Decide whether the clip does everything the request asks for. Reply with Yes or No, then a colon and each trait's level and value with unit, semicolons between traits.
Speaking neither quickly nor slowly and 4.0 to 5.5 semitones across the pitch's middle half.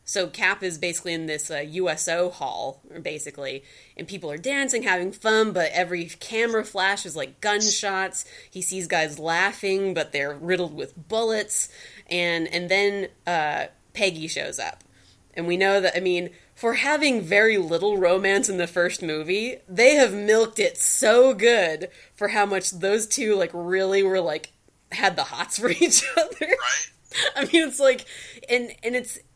Yes: average, 170 wpm; average, 4.3 semitones